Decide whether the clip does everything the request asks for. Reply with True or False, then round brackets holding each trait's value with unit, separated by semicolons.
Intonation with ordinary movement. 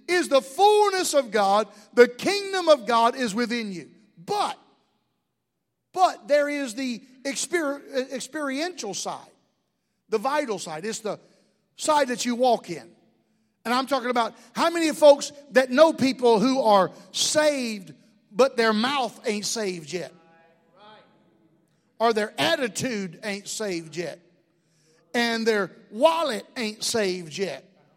False (6.0 semitones)